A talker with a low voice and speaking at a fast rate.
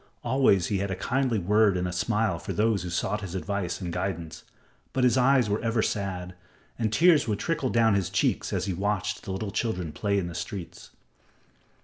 Yes: low, 100 Hz; fast, 210 wpm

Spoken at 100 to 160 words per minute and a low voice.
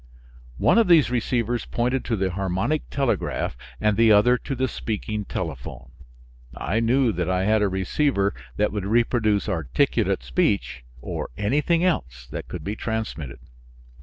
Yes: average, 150 wpm; low, 110 Hz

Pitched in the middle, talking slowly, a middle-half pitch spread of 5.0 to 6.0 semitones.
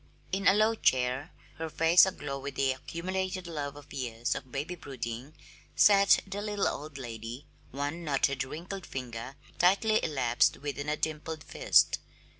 No: medium, 145 Hz; average, 150 wpm; wide, 5.4 semitones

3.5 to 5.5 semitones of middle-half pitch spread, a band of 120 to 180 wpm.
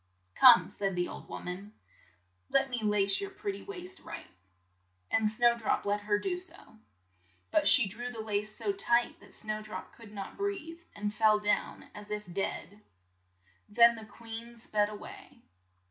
Yes: average, 4.4 semitones; average, 175 wpm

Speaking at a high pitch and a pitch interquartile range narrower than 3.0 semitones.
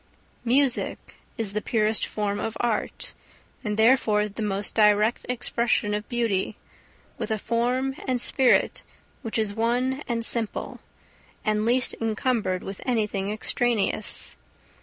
Yes: high, 225 Hz; narrow, 2.5 semitones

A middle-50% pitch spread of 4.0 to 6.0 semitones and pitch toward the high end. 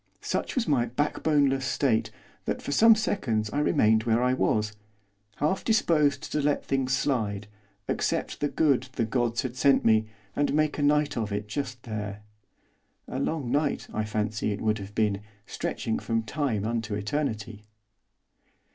No: average, 5.0 semitones; low, 125 Hz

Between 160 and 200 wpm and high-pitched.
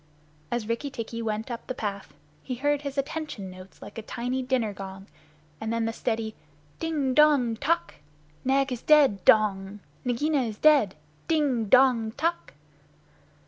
No: average, 150 wpm; high, 240 Hz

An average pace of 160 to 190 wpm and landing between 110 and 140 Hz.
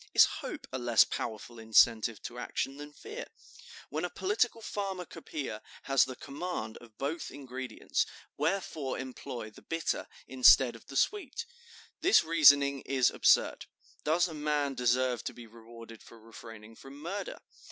No: average, 145 wpm; low, 135 Hz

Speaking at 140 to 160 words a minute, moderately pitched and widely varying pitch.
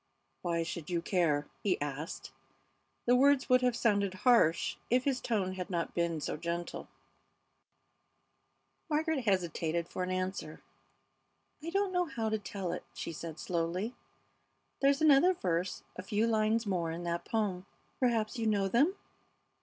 No: average, 150 wpm; high, 195 Hz; wide, 6.0 semitones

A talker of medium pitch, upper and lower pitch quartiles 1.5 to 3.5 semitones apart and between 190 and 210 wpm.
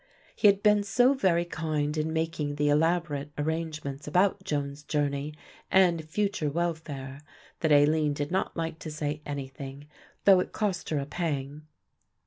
No: medium, 155 Hz; average, 3.0 semitones; average, 150 wpm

